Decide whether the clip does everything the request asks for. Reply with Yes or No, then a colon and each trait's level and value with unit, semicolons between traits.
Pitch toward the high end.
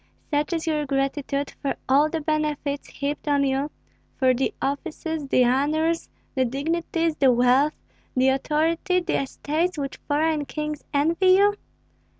Yes: very high, 295 Hz